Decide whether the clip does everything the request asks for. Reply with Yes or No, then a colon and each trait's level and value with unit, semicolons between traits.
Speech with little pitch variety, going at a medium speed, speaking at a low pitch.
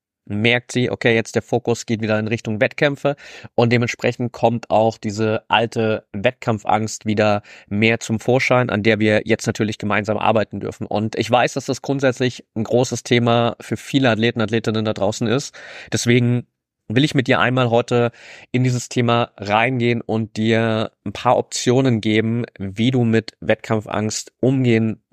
Yes: narrow, 2.0 semitones; average, 160 wpm; low, 115 Hz